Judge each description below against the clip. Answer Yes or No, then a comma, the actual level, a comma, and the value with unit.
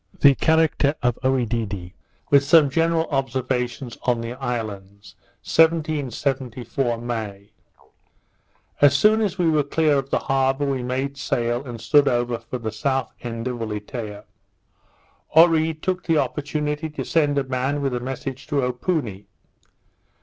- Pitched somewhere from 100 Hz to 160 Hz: Yes, low, 135 Hz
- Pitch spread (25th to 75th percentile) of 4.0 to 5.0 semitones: No, average, 3.6 semitones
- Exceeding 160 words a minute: No, average, 140 wpm